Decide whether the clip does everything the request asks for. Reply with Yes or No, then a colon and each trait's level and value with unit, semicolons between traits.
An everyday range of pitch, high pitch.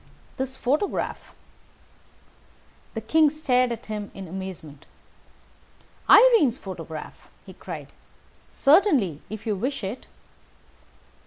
No: wide, 7.1 semitones; high, 235 Hz